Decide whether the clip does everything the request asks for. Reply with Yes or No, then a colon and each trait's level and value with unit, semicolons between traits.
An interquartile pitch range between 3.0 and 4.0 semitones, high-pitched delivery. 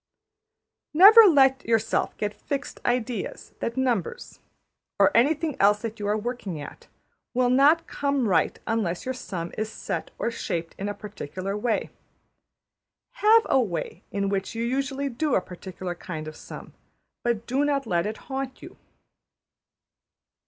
No: wide, 5.5 semitones; high, 230 Hz